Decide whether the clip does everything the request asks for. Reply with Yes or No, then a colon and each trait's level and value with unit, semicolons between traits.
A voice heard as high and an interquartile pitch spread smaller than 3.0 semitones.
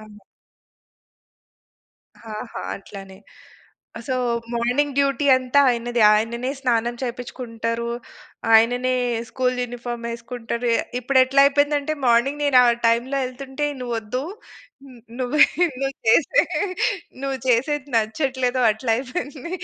Yes: very high, 250 Hz; narrow, 2.6 semitones